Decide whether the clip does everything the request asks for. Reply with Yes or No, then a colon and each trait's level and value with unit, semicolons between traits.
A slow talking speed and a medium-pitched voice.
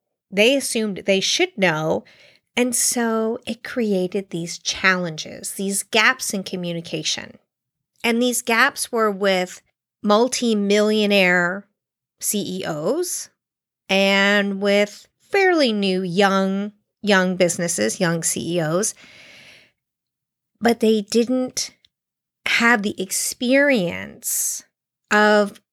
No: slow, 90 wpm; high, 205 Hz